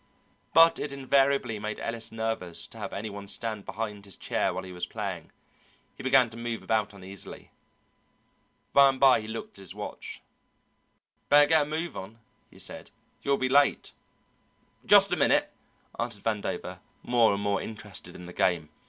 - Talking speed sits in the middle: Yes, average, 170 wpm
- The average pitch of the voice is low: Yes, low, 110 Hz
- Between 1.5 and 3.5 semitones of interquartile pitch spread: No, average, 4.7 semitones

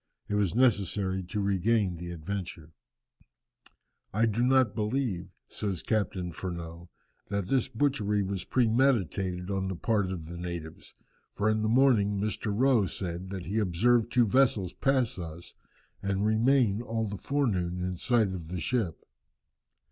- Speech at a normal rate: Yes, average, 150 wpm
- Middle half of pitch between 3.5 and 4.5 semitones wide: Yes, average, 4.1 semitones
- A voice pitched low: Yes, low, 100 Hz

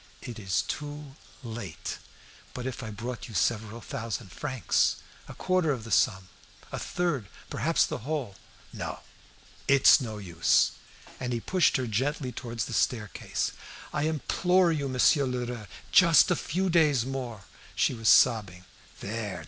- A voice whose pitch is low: Yes, low, 125 Hz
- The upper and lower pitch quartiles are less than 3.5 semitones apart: No, average, 4.9 semitones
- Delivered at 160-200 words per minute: No, average, 150 wpm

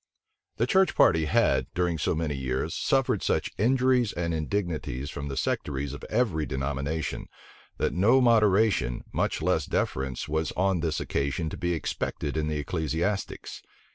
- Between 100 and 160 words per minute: Yes, average, 150 wpm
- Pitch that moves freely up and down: Yes, wide, 5.9 semitones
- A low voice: Yes, very low, 80 Hz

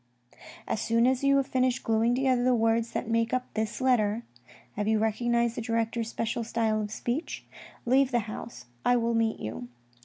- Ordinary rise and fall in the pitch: No, narrow, 1.9 semitones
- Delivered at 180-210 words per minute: Yes, average, 190 wpm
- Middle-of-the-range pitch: No, high, 230 Hz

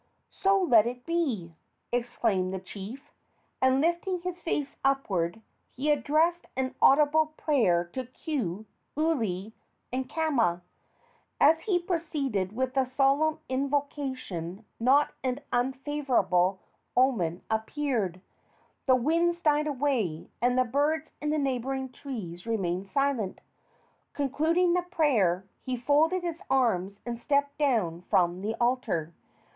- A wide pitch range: Yes, wide, 5.9 semitones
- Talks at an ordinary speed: No, slow, 120 wpm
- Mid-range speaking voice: No, very high, 260 Hz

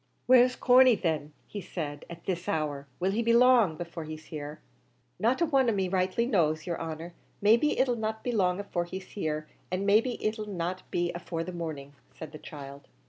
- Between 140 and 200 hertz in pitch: Yes, medium, 185 Hz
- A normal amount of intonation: No, wide, 5.7 semitones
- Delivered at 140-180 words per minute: No, fast, 205 wpm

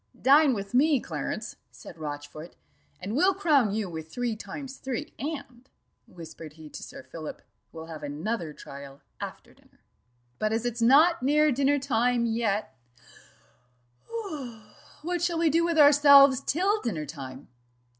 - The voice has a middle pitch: No, high, 240 Hz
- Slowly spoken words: No, average, 145 wpm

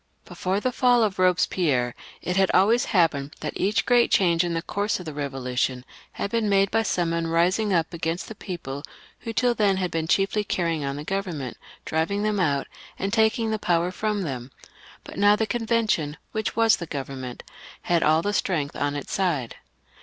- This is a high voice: No, medium, 180 Hz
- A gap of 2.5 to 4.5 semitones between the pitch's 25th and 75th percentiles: No, average, 5.1 semitones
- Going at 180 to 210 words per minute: Yes, average, 190 wpm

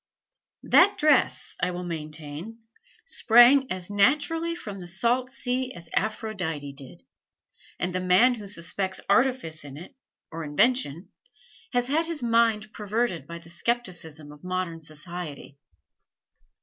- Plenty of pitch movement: Yes, wide, 6.7 semitones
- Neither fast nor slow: No, slow, 130 wpm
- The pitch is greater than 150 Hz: Yes, high, 190 Hz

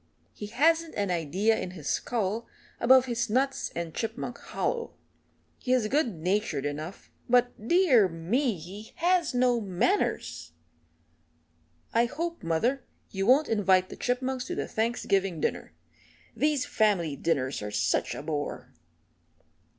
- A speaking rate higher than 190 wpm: No, slow, 135 wpm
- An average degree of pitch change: No, wide, 6.6 semitones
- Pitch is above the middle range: Yes, high, 220 Hz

